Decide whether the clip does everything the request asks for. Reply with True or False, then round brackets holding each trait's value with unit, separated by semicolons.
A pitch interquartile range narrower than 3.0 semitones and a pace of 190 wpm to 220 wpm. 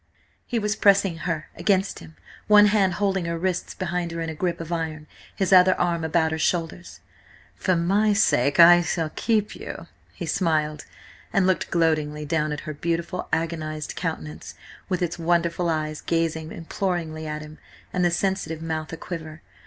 False (2.5 semitones; 175 wpm)